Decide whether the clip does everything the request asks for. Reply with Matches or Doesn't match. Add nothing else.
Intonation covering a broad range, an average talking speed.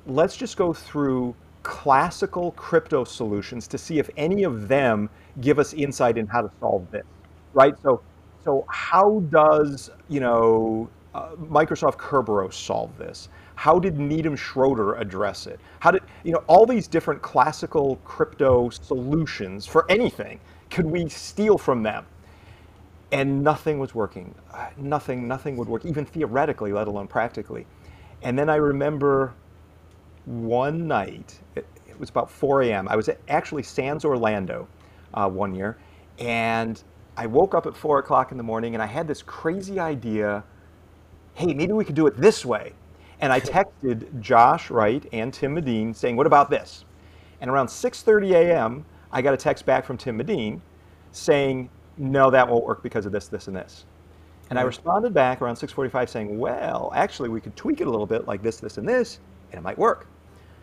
Matches